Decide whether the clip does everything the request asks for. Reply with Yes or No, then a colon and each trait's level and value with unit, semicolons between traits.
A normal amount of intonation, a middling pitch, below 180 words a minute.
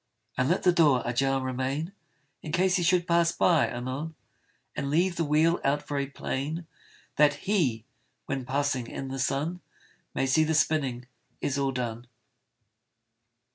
Yes: average, 4.0 semitones; medium, 145 Hz; average, 150 wpm